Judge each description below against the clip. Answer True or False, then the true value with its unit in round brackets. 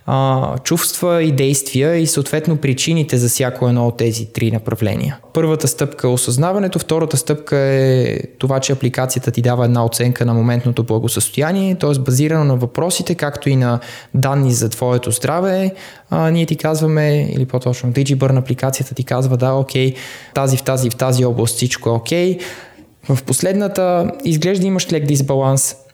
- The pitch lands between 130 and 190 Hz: True (135 Hz)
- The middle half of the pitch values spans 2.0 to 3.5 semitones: False (4.1 semitones)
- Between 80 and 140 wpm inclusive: False (160 wpm)